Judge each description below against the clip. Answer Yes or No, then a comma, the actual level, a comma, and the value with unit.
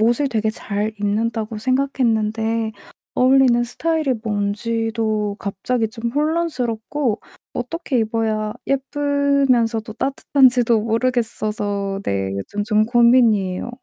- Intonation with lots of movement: No, average, 3.1 semitones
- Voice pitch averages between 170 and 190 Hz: No, high, 230 Hz